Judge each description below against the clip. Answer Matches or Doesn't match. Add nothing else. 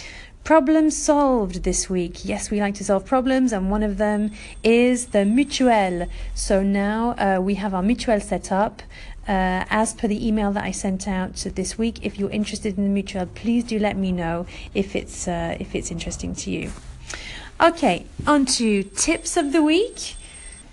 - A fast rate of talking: Doesn't match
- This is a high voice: Matches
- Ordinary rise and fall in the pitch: Matches